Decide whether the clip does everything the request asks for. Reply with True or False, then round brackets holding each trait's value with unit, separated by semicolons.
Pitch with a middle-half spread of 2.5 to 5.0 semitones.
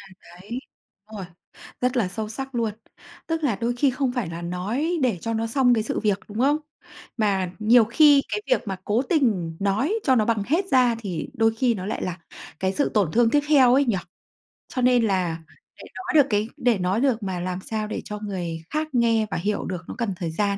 True (4.6 semitones)